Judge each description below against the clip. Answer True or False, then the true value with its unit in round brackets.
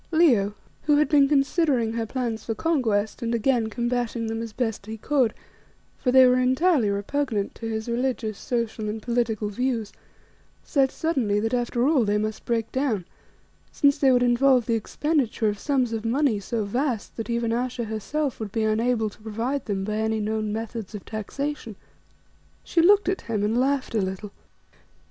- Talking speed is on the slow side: False (175 wpm)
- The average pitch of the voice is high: True (235 Hz)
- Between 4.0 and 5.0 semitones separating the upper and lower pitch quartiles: False (3.4 semitones)